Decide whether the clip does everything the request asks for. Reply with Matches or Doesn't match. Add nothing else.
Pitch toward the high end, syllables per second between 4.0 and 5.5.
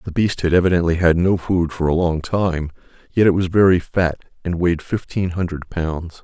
Doesn't match